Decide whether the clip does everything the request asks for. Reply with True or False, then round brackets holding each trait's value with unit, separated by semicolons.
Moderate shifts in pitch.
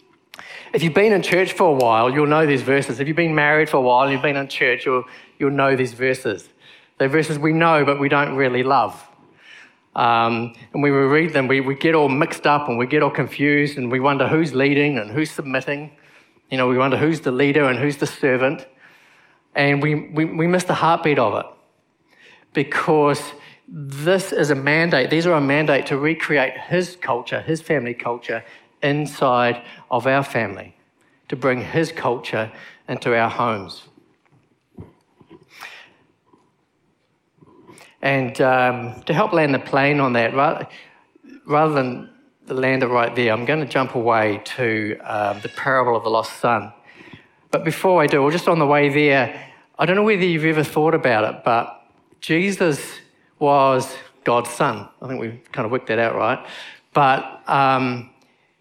True (3.3 semitones)